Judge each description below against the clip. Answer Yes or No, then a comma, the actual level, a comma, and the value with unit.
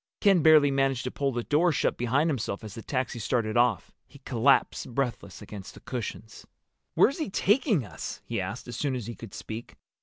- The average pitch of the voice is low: Yes, low, 125 Hz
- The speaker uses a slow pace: No, average, 195 wpm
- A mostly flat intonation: No, average, 4.1 semitones